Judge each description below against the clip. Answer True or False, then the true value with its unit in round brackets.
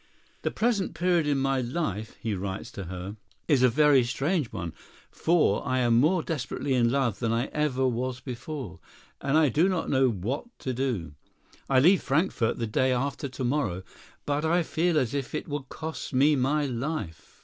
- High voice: False (135 Hz)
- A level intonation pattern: False (4.2 semitones)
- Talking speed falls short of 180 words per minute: False (185 wpm)